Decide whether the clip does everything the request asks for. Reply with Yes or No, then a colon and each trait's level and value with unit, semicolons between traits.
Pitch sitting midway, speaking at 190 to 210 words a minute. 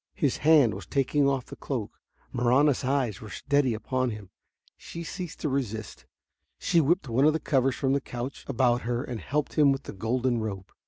No: low, 130 Hz; average, 195 wpm